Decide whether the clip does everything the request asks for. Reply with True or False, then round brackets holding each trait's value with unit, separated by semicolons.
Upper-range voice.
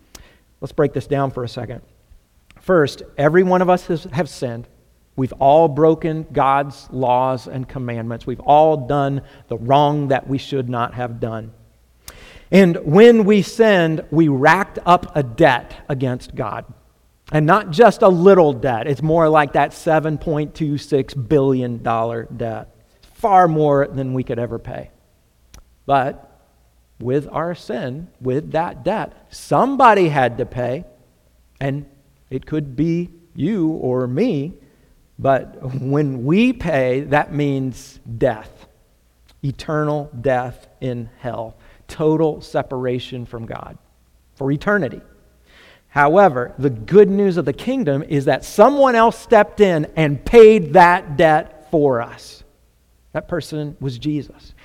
False (140 Hz)